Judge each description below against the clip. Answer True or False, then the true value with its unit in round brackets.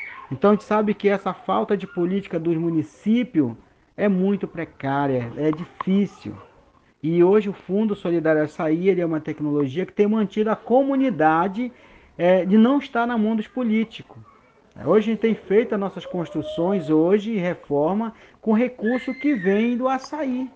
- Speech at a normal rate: True (160 wpm)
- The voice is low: False (200 Hz)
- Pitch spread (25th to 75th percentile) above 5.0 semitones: False (4.6 semitones)